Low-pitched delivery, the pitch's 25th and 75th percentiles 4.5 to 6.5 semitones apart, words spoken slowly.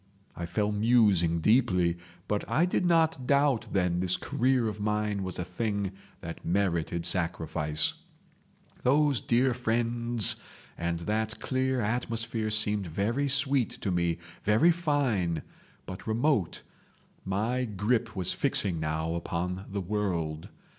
Yes: low, 105 Hz; wide, 5.5 semitones; slow, 125 wpm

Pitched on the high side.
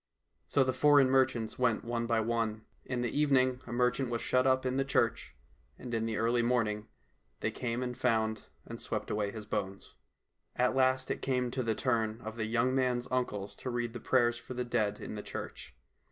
No: low, 120 Hz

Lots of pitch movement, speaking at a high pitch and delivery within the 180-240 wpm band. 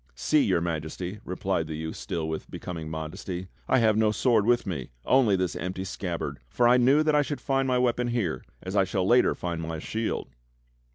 No: wide, 6.5 semitones; very low, 95 Hz; fast, 205 wpm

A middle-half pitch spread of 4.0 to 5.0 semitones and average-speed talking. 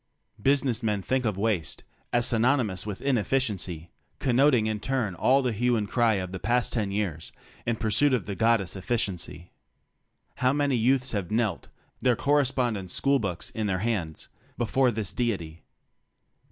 Yes: average, 4.5 semitones; average, 165 wpm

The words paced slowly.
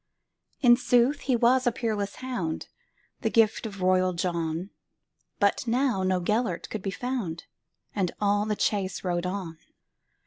Yes: slow, 130 wpm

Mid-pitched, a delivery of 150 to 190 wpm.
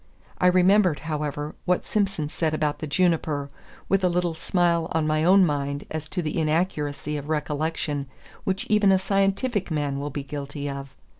Yes: medium, 155 Hz; average, 170 wpm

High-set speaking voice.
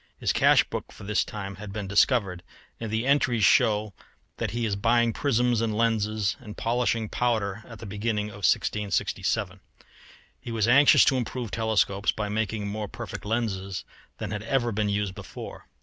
No: low, 110 Hz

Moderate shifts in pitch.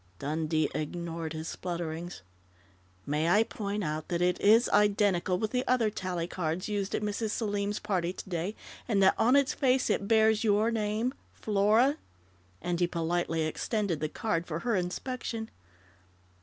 Yes: average, 4.3 semitones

